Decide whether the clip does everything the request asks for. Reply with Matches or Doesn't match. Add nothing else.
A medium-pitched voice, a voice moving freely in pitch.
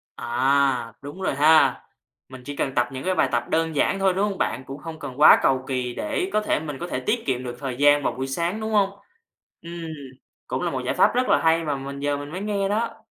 Matches